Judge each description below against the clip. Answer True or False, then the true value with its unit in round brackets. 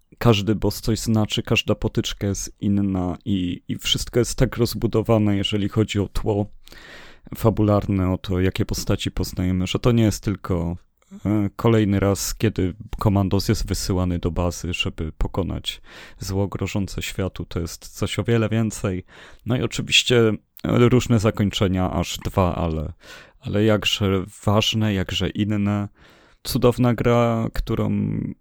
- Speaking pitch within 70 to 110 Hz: True (100 Hz)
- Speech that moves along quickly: False (135 wpm)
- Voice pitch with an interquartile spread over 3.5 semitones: False (3.2 semitones)